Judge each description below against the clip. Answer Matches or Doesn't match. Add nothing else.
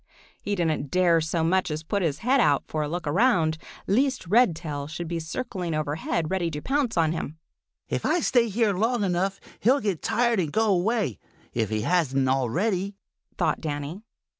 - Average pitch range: Doesn't match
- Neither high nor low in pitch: Matches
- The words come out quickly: Doesn't match